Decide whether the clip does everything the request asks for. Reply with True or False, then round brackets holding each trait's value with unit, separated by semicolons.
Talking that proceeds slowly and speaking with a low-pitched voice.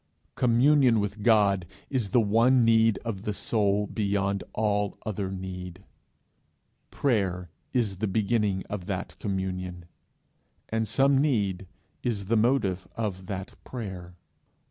True (120 wpm; 105 Hz)